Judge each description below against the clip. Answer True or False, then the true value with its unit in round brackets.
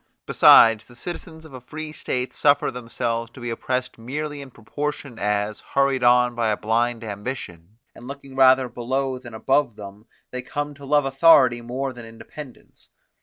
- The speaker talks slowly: False (170 wpm)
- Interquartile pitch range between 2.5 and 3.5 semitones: True (3.1 semitones)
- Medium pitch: False (125 Hz)